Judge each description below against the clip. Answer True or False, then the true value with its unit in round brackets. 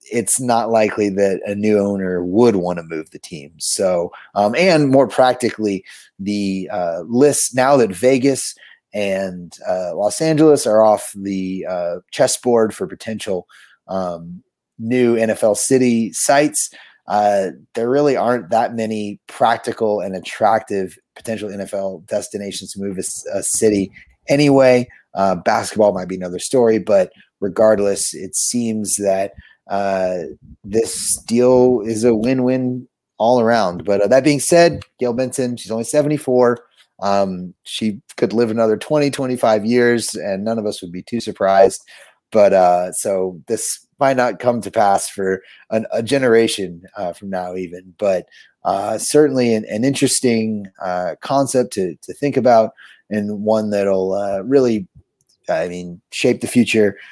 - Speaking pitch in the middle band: False (110 Hz)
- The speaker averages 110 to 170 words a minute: True (150 wpm)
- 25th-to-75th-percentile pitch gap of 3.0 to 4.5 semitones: True (4.1 semitones)